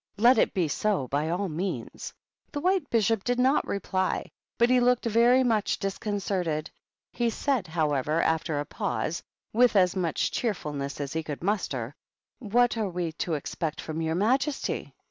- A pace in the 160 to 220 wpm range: Yes, average, 165 wpm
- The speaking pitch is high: Yes, high, 195 Hz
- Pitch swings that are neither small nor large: No, wide, 6.7 semitones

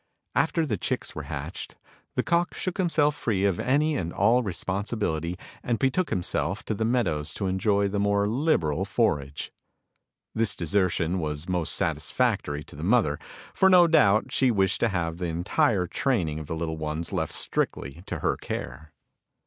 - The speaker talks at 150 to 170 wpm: Yes, average, 165 wpm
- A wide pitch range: Yes, wide, 6.8 semitones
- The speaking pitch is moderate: No, low, 100 Hz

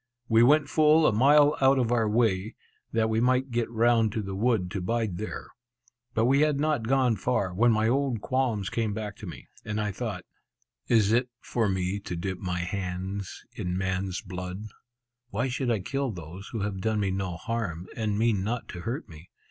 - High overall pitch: No, low, 110 Hz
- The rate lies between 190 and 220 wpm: Yes, average, 200 wpm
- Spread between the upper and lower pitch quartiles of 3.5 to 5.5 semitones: Yes, average, 4.2 semitones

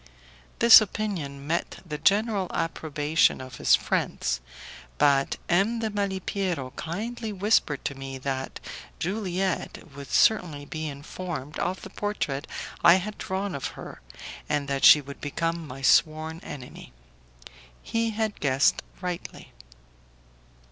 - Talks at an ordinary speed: No, slow, 125 wpm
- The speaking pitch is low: No, medium, 165 Hz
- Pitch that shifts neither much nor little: No, wide, 5.9 semitones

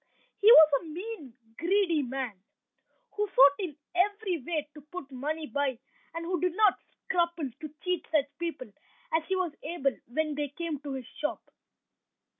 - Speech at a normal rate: Yes, average, 165 wpm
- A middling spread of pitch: Yes, average, 4.1 semitones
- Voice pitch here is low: No, very high, 315 Hz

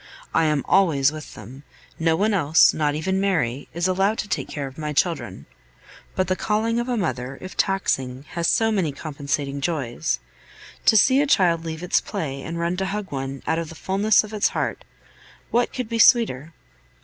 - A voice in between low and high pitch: Yes, medium, 165 Hz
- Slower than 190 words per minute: No, average, 195 wpm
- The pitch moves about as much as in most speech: No, wide, 5.7 semitones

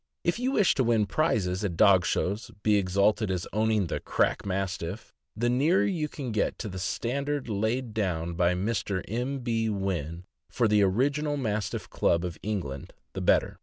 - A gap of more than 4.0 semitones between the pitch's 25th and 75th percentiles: Yes, average, 4.8 semitones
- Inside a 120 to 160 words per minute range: No, average, 180 wpm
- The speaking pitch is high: No, low, 105 Hz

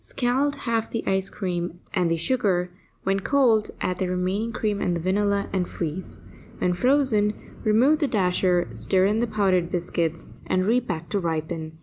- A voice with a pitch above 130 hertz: Yes, high, 190 Hz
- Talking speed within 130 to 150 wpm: No, average, 160 wpm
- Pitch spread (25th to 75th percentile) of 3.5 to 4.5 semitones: Yes, average, 3.9 semitones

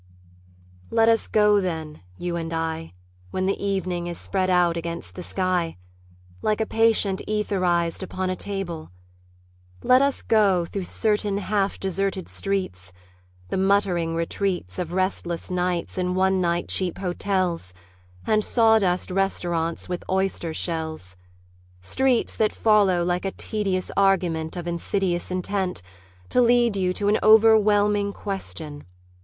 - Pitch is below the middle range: No, medium, 185 Hz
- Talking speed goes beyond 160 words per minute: No, slow, 135 wpm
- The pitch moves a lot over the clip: No, average, 2.9 semitones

